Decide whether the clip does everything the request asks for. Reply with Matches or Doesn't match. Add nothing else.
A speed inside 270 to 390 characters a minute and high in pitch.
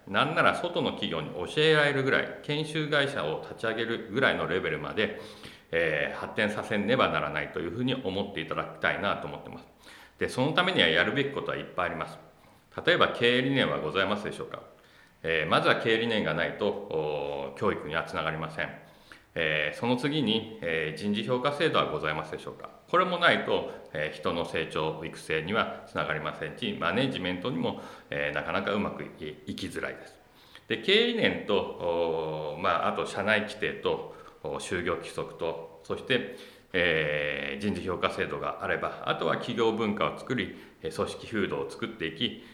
Doesn't match